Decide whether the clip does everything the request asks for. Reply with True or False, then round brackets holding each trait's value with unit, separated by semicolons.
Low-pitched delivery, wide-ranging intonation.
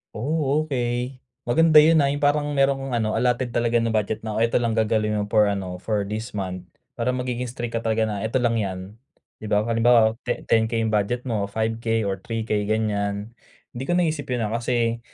False (115 Hz; 2.6 semitones)